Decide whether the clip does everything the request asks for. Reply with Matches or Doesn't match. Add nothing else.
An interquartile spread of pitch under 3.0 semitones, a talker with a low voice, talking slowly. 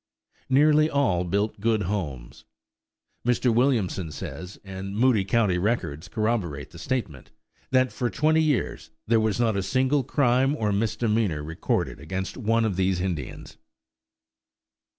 Doesn't match